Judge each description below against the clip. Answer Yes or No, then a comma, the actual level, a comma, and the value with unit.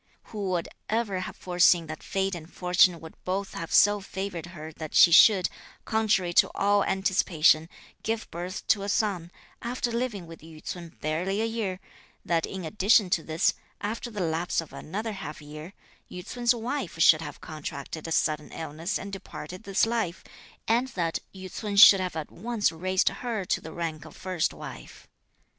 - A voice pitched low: No, medium, 185 Hz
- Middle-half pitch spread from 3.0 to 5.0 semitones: Yes, average, 3.9 semitones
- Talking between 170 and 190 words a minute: Yes, average, 180 wpm